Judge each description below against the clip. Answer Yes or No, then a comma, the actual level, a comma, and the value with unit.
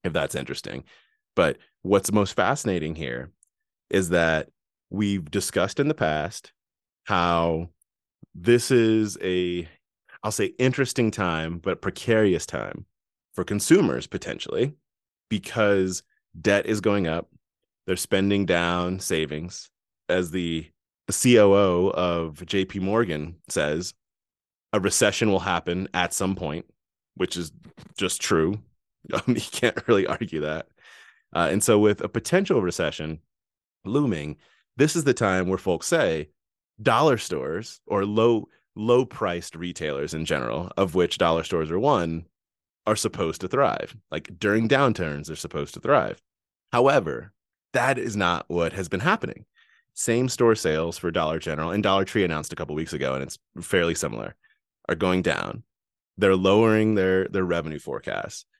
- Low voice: Yes, very low, 95 Hz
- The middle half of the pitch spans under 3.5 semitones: No, average, 3.9 semitones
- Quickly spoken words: No, average, 140 wpm